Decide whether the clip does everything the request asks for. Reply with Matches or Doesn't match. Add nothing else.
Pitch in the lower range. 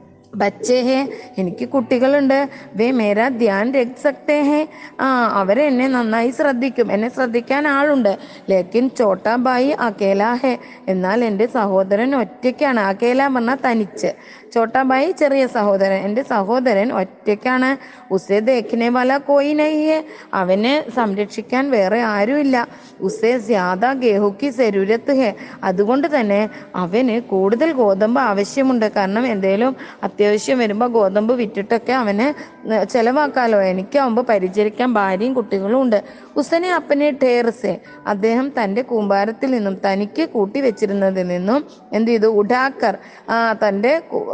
Doesn't match